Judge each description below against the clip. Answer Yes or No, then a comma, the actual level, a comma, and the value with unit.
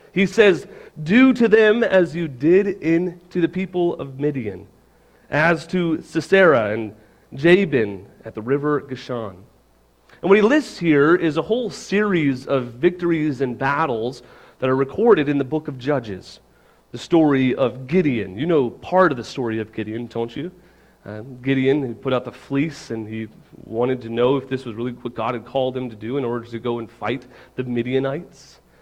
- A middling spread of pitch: No, wide, 6.1 semitones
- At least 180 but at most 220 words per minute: Yes, average, 185 wpm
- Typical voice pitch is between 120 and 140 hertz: Yes, low, 135 Hz